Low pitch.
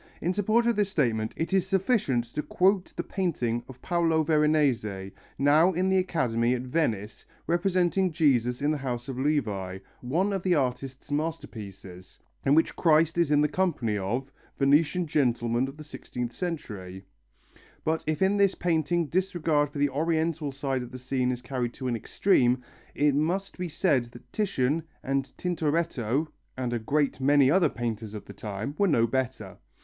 No: medium, 145 Hz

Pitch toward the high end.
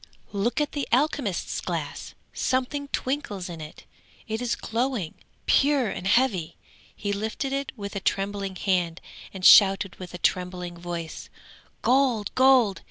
Yes: high, 205 Hz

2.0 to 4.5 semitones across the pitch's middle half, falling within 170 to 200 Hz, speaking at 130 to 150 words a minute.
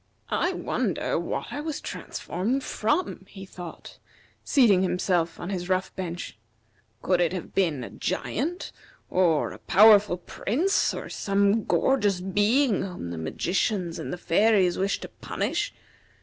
Yes: average, 3.3 semitones; high, 190 Hz; average, 140 wpm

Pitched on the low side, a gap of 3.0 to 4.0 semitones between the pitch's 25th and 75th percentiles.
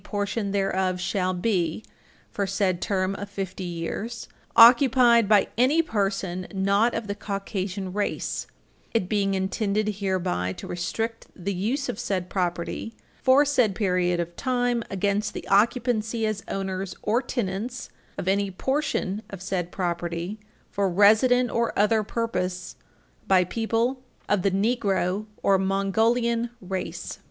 No: high, 200 Hz; average, 3.4 semitones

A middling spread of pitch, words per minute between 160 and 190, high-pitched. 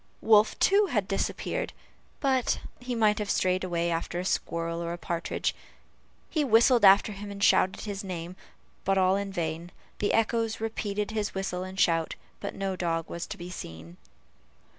Yes: average, 3.7 semitones; average, 165 wpm; high, 195 Hz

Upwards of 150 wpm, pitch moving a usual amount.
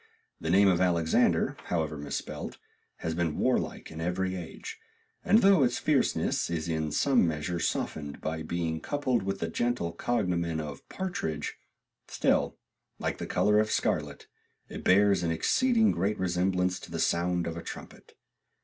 Yes: average, 160 wpm; average, 4.5 semitones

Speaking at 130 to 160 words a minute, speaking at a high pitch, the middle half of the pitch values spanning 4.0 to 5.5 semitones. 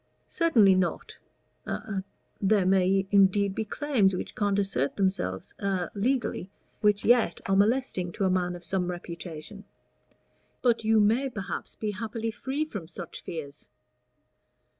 No: average, 140 wpm; high, 195 Hz; average, 3.2 semitones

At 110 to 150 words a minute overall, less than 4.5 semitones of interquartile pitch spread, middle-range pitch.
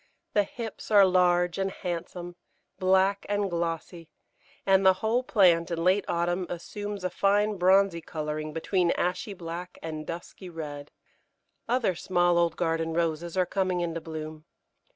Yes: average, 145 wpm; narrow, 2.5 semitones; medium, 175 Hz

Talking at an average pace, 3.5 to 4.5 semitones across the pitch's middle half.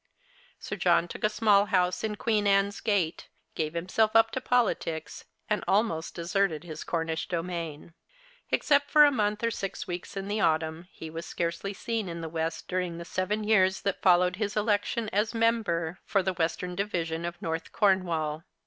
Yes: average, 175 wpm; average, 3.9 semitones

